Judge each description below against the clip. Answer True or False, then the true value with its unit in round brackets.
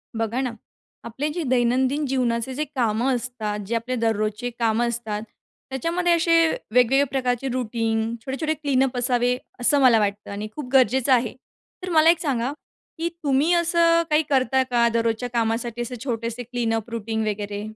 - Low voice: False (245 Hz)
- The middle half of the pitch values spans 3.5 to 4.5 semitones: False (3.1 semitones)